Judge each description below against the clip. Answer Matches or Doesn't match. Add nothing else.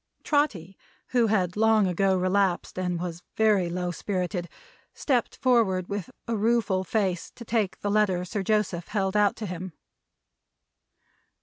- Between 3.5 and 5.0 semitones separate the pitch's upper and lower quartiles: Doesn't match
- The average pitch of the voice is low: Doesn't match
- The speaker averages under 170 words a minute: Matches